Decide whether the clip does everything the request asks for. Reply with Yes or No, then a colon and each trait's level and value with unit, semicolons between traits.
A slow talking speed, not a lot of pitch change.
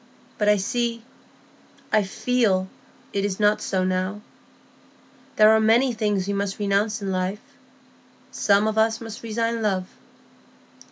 Yes: slow, 125 wpm; narrow, 2.1 semitones